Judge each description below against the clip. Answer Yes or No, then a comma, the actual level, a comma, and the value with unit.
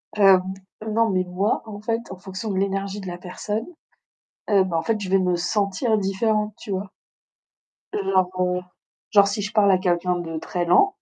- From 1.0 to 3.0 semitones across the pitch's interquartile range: Yes, narrow, 2.5 semitones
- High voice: Yes, high, 195 Hz